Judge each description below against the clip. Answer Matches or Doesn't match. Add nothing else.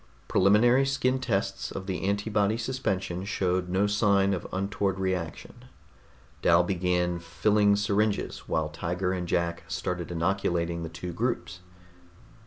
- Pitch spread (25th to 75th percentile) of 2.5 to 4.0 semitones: Matches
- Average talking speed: Doesn't match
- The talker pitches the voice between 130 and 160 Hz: Doesn't match